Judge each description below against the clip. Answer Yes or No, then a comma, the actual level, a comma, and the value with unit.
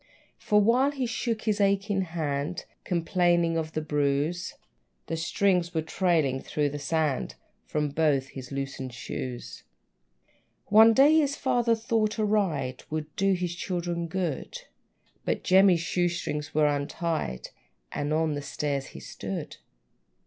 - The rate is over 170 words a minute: No, average, 140 wpm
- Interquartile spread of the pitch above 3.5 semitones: Yes, average, 5.1 semitones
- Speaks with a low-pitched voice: No, medium, 170 Hz